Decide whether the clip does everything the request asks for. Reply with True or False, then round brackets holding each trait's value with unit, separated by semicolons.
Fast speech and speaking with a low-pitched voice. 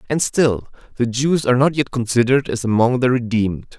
False (190 wpm; 120 Hz)